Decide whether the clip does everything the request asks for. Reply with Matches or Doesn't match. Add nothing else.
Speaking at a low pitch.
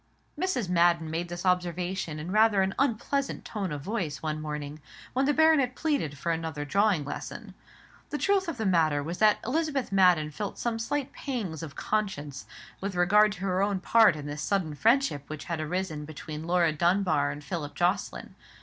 Doesn't match